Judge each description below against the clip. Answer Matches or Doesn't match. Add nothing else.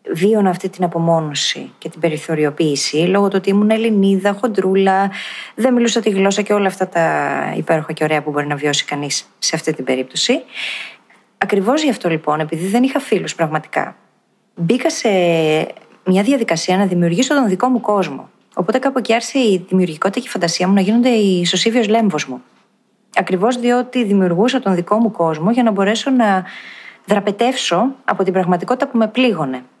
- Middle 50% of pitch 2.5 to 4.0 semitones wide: Doesn't match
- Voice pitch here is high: Matches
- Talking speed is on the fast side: Matches